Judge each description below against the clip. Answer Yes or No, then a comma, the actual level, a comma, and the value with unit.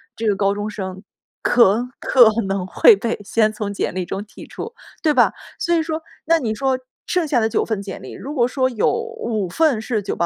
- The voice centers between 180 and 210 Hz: No, high, 230 Hz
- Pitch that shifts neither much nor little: No, wide, 6.3 semitones